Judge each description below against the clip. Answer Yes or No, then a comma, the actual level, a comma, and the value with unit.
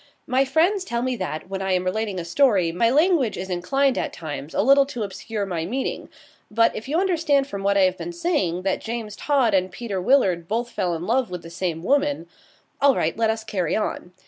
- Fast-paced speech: Yes, fast, 225 wpm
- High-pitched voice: Yes, high, 220 Hz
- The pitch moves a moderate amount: No, wide, 6.8 semitones